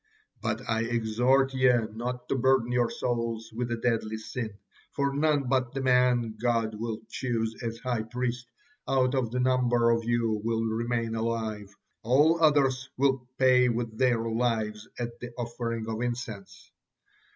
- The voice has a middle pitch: No, low, 120 Hz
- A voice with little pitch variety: Yes, narrow, 2.0 semitones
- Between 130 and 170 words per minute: Yes, average, 155 wpm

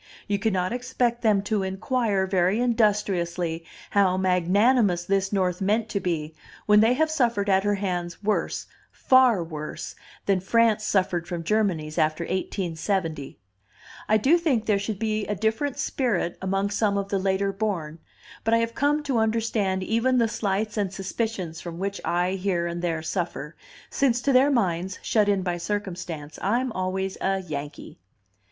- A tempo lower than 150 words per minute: No, average, 160 wpm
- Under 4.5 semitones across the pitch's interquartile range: Yes, average, 3.6 semitones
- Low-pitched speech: No, high, 195 Hz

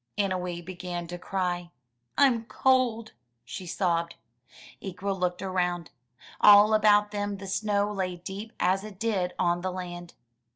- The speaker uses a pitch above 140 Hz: Yes, high, 190 Hz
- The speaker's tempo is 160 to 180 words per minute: No, slow, 135 wpm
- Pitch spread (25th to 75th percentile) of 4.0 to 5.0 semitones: No, narrow, 2.6 semitones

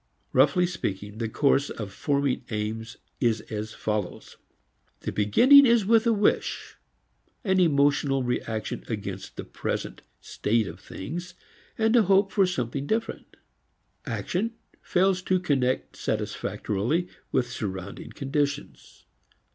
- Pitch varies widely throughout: Yes, wide, 8.9 semitones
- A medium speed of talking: No, slow, 120 wpm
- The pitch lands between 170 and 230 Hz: No, medium, 140 Hz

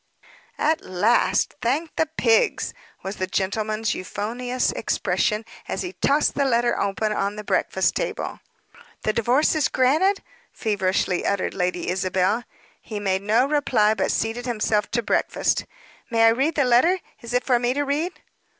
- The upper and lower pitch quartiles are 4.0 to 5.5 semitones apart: Yes, average, 4.4 semitones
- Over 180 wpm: No, average, 155 wpm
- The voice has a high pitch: Yes, high, 230 Hz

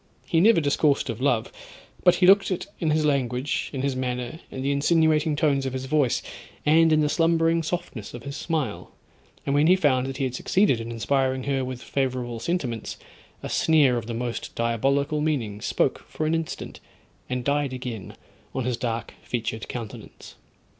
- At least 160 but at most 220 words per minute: Yes, average, 180 wpm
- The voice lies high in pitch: No, low, 135 Hz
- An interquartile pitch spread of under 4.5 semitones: Yes, average, 4.0 semitones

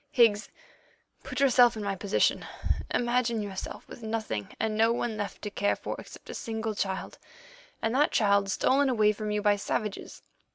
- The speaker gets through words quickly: No, average, 170 wpm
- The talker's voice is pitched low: No, high, 215 Hz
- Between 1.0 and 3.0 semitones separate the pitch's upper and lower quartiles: Yes, narrow, 2.4 semitones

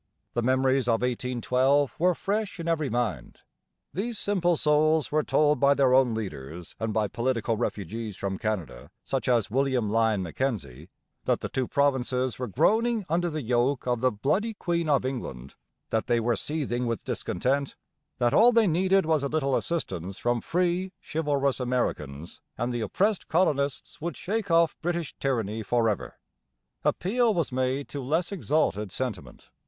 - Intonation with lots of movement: Yes, wide, 6.0 semitones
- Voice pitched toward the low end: Yes, low, 130 Hz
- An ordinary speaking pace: Yes, average, 160 wpm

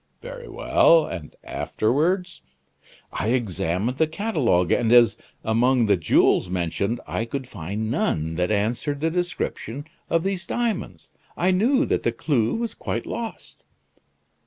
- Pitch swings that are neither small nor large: No, wide, 8.8 semitones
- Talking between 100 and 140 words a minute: Yes, slow, 135 wpm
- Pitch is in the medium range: No, low, 125 Hz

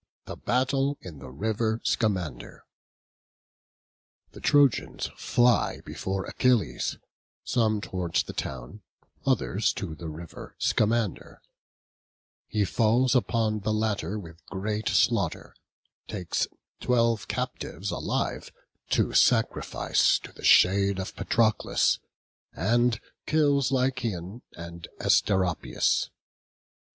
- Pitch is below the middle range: Yes, low, 105 Hz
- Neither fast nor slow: No, slow, 100 wpm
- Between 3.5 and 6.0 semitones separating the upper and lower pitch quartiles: Yes, average, 4.8 semitones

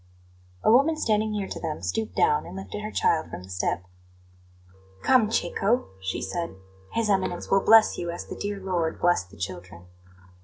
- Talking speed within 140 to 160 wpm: No, average, 180 wpm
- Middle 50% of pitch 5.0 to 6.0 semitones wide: Yes, wide, 5.5 semitones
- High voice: Yes, high, 195 Hz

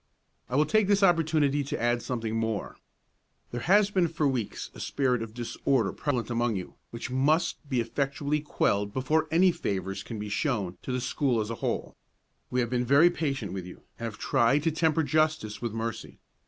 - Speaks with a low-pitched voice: Yes, low, 130 Hz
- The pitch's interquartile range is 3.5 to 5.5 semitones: Yes, average, 5.2 semitones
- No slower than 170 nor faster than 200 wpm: Yes, average, 195 wpm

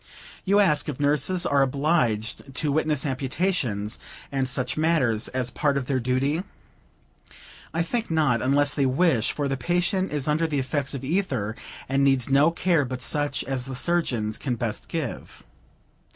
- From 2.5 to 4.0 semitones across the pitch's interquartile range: Yes, average, 3.7 semitones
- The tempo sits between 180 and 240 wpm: No, average, 165 wpm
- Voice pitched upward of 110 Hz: Yes, medium, 140 Hz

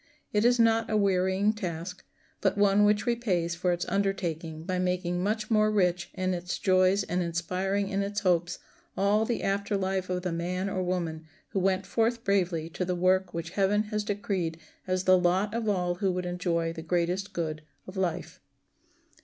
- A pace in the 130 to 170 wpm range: No, average, 185 wpm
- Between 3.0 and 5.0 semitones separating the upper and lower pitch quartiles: No, narrow, 2.4 semitones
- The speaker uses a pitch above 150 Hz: Yes, medium, 185 Hz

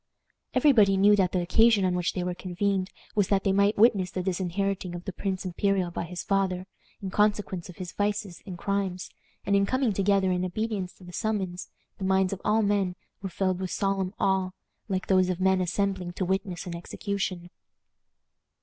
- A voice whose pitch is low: No, high, 190 Hz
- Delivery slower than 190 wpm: No, average, 195 wpm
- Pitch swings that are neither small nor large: No, narrow, 1.7 semitones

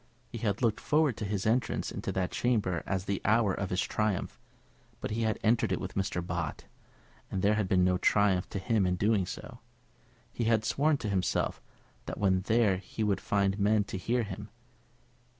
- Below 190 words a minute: No, average, 195 wpm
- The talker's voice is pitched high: No, low, 105 Hz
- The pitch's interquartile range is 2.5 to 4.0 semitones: Yes, average, 2.8 semitones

